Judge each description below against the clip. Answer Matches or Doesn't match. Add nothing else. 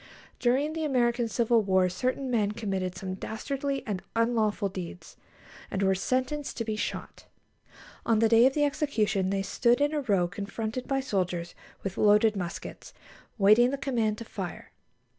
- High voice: Matches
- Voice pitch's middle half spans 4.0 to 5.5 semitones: Matches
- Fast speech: Doesn't match